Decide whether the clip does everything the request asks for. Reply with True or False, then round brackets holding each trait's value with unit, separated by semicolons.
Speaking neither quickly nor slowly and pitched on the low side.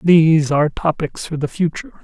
False (175 wpm; 160 Hz)